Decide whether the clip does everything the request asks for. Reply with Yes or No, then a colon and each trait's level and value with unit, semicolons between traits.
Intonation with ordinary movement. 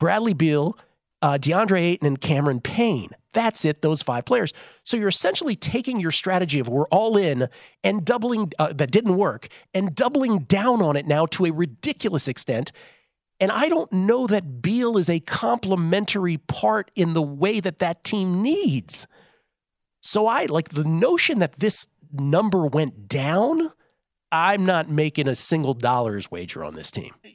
No: wide, 5.9 semitones